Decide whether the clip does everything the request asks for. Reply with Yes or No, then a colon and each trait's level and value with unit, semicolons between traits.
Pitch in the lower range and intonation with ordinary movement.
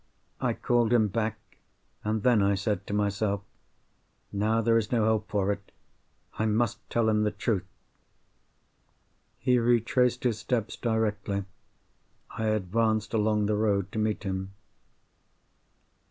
No: low, 110 Hz; narrow, 1.9 semitones